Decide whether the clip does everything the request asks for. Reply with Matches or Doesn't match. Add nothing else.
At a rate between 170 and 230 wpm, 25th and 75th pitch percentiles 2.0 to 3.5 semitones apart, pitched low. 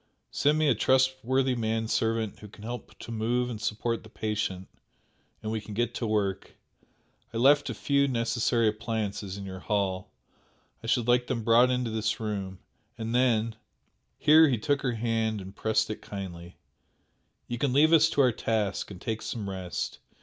Matches